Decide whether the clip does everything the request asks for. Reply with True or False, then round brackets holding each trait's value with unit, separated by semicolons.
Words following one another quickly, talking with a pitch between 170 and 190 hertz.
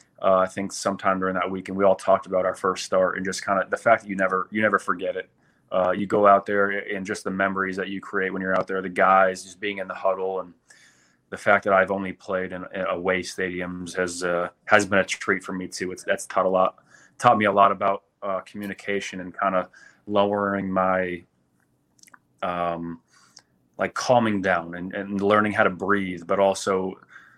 False (220 wpm; 95 Hz)